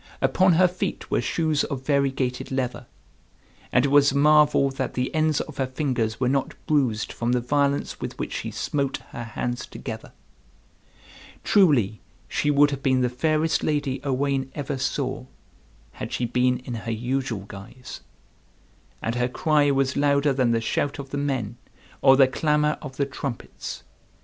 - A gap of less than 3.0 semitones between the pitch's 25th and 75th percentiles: Yes, narrow, 2.5 semitones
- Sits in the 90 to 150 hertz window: Yes, low, 135 Hz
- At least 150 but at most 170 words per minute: Yes, average, 165 wpm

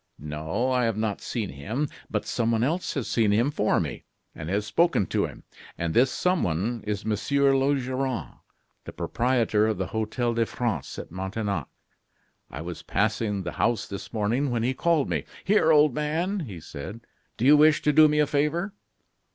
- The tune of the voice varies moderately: No, wide, 5.7 semitones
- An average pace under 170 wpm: No, average, 180 wpm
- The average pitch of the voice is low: Yes, low, 115 Hz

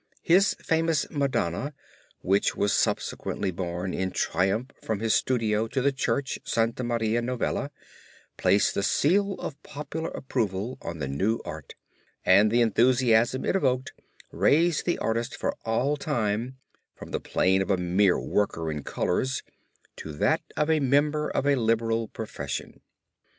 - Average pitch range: No, wide, 5.8 semitones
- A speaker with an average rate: Yes, average, 150 wpm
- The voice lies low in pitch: Yes, low, 115 Hz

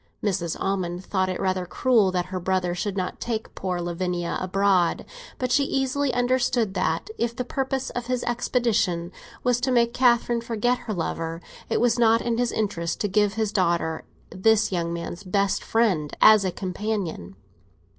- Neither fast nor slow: Yes, average, 170 wpm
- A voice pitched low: No, high, 205 Hz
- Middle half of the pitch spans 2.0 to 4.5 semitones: No, average, 4.9 semitones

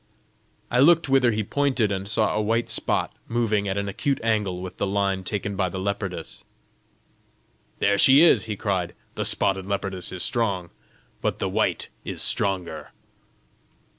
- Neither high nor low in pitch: No, low, 100 Hz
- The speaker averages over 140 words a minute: Yes, average, 160 wpm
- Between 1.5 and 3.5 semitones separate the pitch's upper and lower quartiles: Yes, average, 3.1 semitones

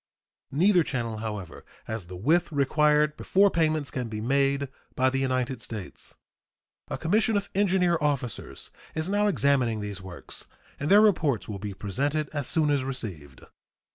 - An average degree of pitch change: No, wide, 6.2 semitones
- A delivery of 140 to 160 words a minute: Yes, average, 155 wpm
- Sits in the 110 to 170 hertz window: Yes, medium, 140 Hz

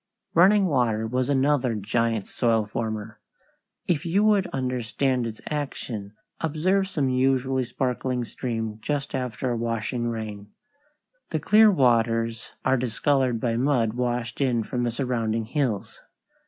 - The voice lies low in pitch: Yes, low, 125 Hz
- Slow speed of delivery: Yes, slow, 130 wpm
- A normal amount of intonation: Yes, average, 3.1 semitones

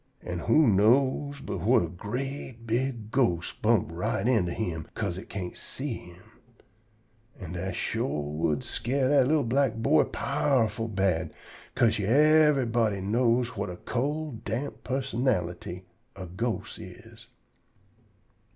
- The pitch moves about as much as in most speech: No, wide, 6.1 semitones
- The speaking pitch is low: Yes, low, 115 Hz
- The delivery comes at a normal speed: No, slow, 130 wpm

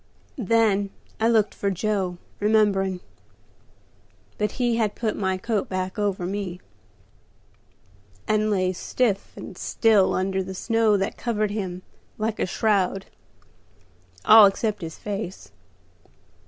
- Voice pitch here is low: No, high, 205 Hz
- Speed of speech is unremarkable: No, slow, 120 wpm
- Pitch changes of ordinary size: No, narrow, 2.3 semitones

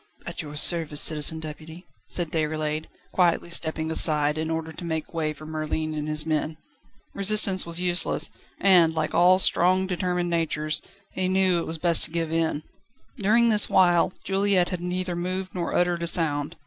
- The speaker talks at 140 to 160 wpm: No, average, 175 wpm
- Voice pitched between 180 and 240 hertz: No, medium, 170 Hz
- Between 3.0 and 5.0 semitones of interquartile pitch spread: No, narrow, 2.5 semitones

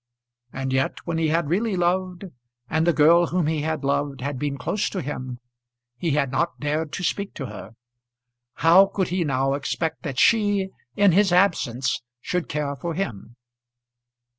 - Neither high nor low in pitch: Yes, medium, 160 Hz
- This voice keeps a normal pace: Yes, average, 170 wpm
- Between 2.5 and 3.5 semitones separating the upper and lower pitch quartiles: No, average, 4.5 semitones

